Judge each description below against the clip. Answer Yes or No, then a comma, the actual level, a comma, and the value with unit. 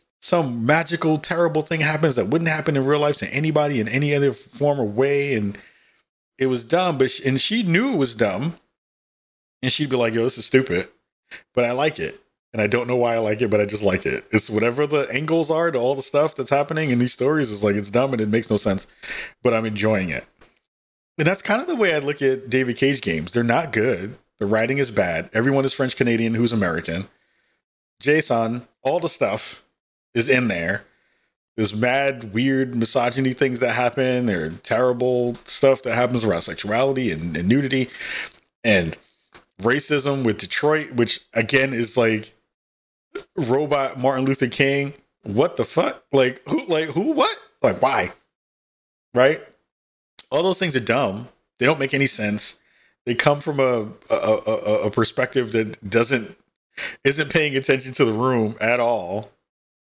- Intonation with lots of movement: No, average, 4.0 semitones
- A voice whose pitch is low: Yes, low, 130 Hz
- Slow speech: No, average, 185 wpm